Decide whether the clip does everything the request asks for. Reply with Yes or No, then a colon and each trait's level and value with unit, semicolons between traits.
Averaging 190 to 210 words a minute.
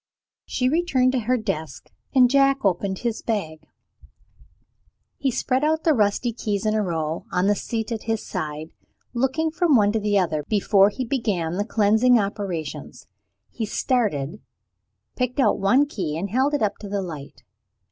No: average, 165 wpm